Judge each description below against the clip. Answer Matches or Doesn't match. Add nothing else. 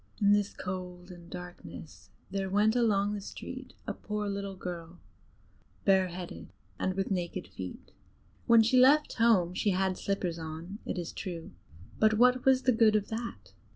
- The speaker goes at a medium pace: Matches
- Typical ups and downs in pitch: Matches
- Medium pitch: Doesn't match